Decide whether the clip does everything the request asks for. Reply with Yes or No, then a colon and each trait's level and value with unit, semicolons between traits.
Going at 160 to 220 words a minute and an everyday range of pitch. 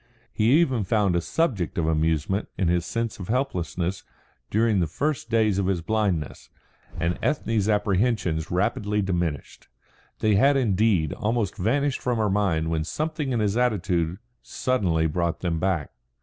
No: average, 150 wpm; average, 4.9 semitones